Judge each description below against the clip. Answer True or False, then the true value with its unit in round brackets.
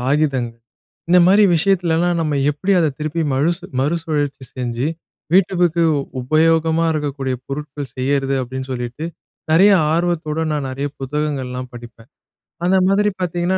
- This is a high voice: False (150 Hz)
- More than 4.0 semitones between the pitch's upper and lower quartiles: True (4.4 semitones)